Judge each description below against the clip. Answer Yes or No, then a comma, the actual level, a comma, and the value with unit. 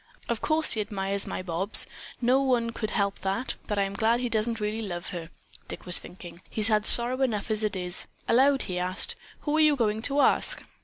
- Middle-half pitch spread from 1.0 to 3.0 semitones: No, average, 3.7 semitones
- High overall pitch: Yes, high, 215 Hz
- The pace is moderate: No, fast, 215 wpm